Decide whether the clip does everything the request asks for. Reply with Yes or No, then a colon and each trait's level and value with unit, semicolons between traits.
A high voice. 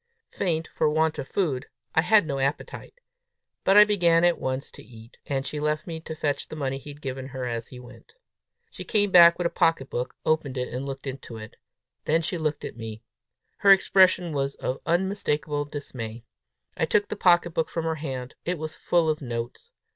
No: medium, 150 Hz